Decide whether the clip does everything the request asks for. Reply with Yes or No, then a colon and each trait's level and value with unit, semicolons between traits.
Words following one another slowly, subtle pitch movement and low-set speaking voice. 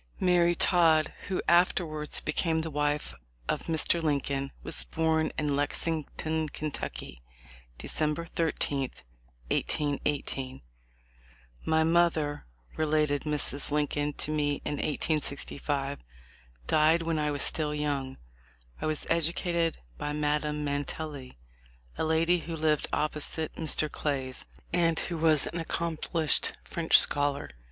No: slow, 115 wpm; narrow, 2.0 semitones; medium, 150 Hz